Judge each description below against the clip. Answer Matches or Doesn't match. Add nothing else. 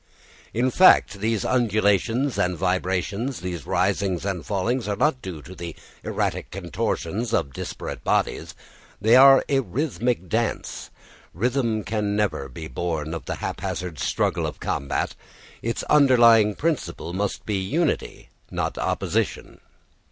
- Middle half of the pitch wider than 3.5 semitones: Matches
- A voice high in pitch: Doesn't match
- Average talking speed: Doesn't match